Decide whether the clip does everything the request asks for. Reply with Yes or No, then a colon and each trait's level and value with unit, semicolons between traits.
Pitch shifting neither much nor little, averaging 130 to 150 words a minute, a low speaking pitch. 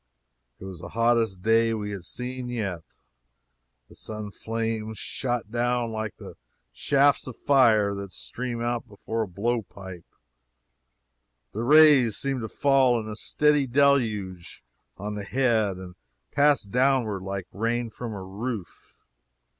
Yes: average, 3.5 semitones; average, 140 wpm; low, 115 Hz